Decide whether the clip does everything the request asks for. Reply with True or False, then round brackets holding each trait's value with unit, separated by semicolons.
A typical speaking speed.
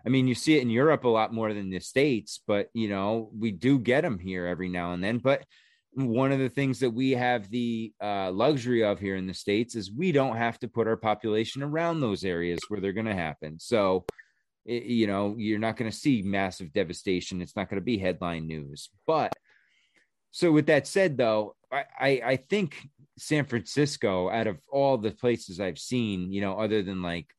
False (215 wpm)